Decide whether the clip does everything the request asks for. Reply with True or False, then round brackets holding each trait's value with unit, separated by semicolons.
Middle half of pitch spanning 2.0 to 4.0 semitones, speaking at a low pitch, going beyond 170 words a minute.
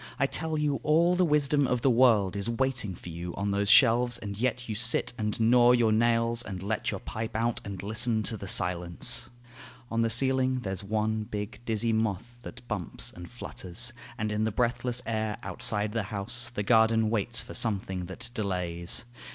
True (3.1 semitones; 110 Hz; 190 wpm)